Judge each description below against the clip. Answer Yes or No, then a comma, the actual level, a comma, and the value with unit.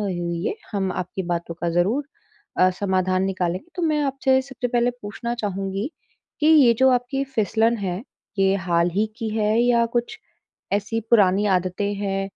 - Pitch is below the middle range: No, high, 205 Hz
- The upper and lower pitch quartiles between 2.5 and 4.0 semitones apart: No, average, 4.5 semitones